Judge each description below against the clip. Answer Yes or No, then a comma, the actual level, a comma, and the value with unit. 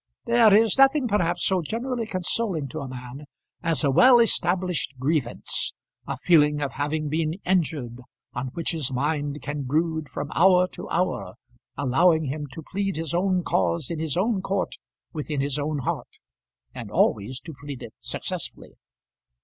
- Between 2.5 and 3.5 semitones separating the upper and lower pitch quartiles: No, average, 4.5 semitones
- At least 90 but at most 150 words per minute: No, average, 160 wpm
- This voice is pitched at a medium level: Yes, medium, 160 Hz